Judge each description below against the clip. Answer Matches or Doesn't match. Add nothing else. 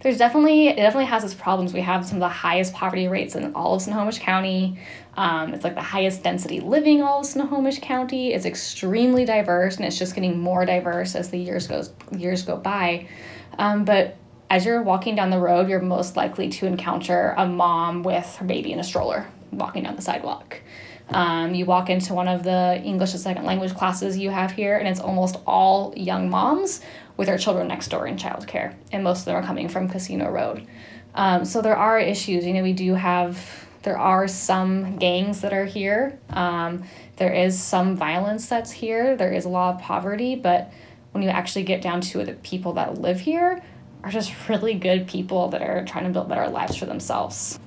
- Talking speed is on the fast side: Matches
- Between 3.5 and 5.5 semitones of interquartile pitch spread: Doesn't match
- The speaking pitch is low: Doesn't match